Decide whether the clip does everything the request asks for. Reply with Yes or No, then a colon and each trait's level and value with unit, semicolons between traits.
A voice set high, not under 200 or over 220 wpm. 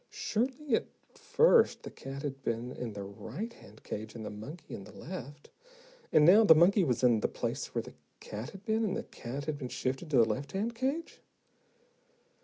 No: medium, 145 Hz; fast, 205 wpm